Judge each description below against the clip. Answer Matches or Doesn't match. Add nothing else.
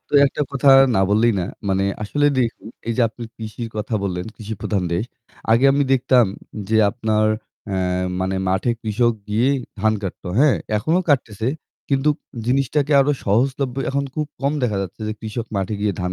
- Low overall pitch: Matches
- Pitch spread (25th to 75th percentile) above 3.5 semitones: Matches